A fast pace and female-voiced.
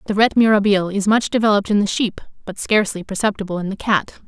Yes: fast, 210 wpm; female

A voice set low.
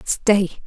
No: high, 195 Hz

